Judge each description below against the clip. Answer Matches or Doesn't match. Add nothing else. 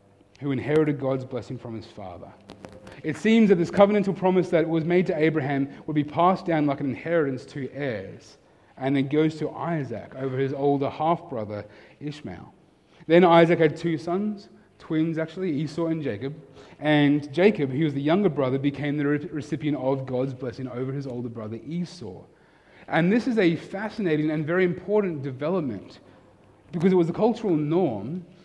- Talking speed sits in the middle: Matches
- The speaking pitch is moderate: Matches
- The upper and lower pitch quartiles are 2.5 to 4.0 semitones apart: Doesn't match